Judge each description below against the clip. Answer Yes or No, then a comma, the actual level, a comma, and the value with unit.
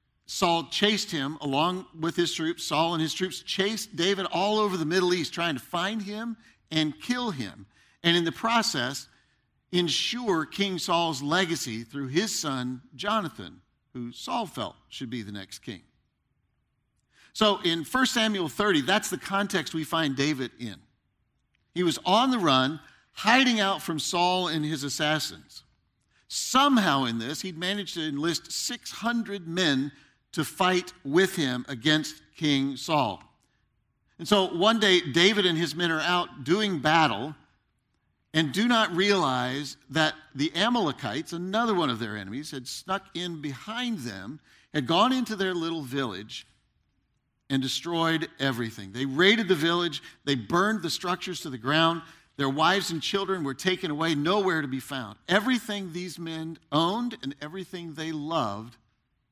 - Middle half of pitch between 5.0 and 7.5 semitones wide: Yes, wide, 5.4 semitones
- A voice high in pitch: No, medium, 165 Hz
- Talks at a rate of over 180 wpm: No, average, 155 wpm